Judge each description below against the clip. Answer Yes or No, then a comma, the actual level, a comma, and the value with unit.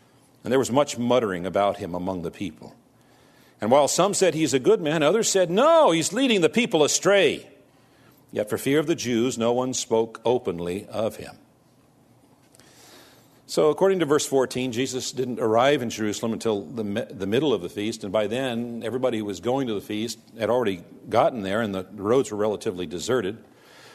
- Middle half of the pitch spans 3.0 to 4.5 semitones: No, average, 5.2 semitones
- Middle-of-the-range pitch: No, low, 125 Hz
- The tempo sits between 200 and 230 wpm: No, average, 190 wpm